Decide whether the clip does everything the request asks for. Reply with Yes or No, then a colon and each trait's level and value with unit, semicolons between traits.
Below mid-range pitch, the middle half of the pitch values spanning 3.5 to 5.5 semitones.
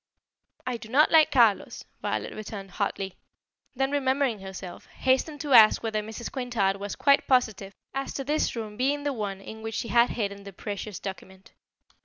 No: high, 225 Hz; average, 4.9 semitones